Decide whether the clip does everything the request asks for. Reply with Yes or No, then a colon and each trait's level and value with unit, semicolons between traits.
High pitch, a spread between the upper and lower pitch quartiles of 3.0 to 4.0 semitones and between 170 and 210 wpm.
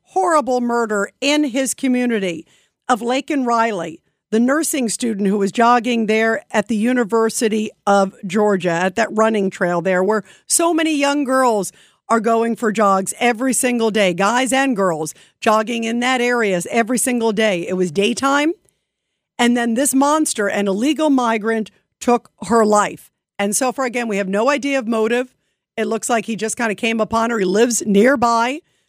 Yes: high, 230 Hz; average, 3.7 semitones; average, 175 wpm